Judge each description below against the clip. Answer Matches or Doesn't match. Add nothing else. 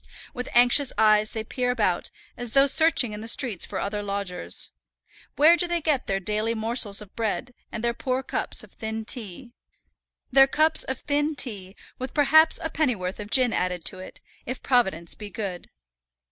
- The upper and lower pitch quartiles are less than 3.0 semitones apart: Doesn't match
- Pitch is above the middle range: Matches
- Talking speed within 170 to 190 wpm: Matches